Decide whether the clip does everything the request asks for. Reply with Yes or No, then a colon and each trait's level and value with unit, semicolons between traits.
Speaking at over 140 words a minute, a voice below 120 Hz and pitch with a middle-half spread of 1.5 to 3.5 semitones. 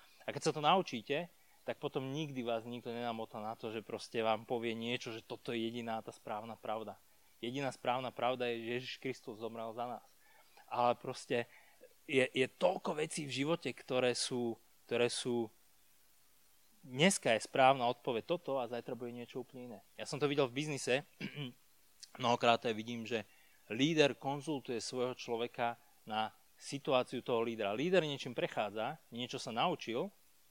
No: average, 160 wpm; low, 125 Hz; average, 2.8 semitones